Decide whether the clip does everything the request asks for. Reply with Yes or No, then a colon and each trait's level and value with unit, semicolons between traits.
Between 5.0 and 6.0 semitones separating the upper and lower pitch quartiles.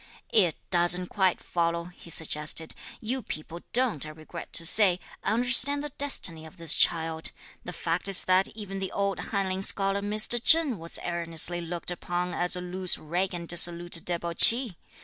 No: average, 2.9 semitones